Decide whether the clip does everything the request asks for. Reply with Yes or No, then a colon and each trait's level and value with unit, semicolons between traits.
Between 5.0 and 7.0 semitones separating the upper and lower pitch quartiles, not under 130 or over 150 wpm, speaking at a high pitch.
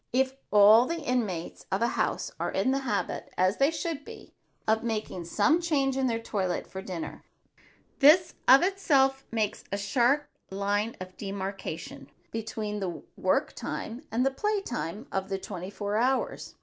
No: average, 5.3 semitones; average, 165 wpm; high, 225 Hz